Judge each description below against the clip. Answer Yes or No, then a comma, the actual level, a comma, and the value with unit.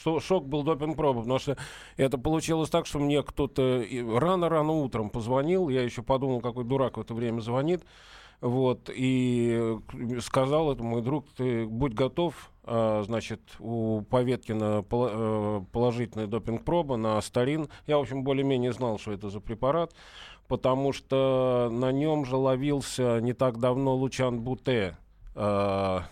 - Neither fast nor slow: Yes, average, 135 wpm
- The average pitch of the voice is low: Yes, low, 125 Hz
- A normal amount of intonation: Yes, average, 3.1 semitones